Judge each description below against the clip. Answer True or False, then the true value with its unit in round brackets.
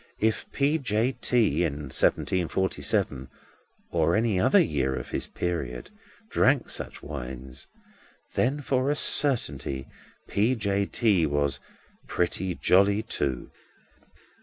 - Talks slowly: True (120 wpm)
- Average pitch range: False (7.9 semitones)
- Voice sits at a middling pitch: False (95 Hz)